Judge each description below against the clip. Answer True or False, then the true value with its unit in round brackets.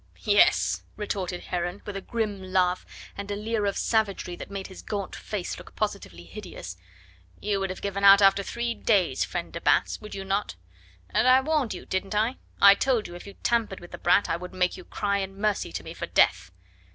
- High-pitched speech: True (200 Hz)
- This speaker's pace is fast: True (210 wpm)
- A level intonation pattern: True (2.2 semitones)